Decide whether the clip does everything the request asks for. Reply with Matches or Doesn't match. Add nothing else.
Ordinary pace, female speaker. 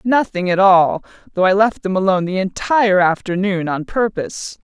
Matches